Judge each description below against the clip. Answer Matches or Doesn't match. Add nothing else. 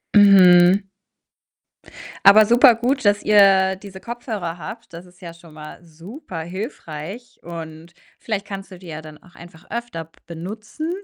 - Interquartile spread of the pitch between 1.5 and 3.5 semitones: Doesn't match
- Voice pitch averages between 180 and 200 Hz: Matches